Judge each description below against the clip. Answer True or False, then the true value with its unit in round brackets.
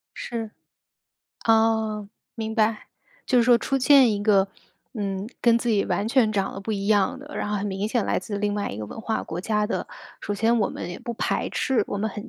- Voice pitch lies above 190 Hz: True (215 Hz)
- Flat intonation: True (2.3 semitones)